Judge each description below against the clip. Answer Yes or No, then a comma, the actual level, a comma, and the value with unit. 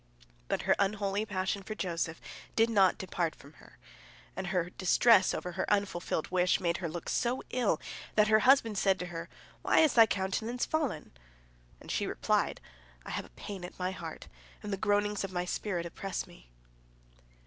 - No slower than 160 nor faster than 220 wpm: Yes, average, 180 wpm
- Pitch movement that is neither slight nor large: Yes, average, 3.2 semitones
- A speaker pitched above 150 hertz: Yes, high, 190 Hz